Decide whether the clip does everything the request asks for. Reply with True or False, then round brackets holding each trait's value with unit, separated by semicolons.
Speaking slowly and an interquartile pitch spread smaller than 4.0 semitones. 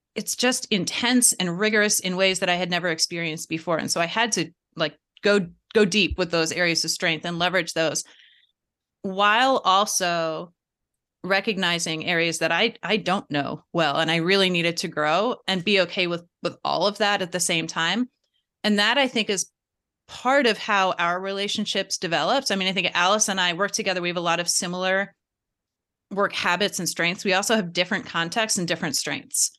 False (195 wpm; 3.3 semitones)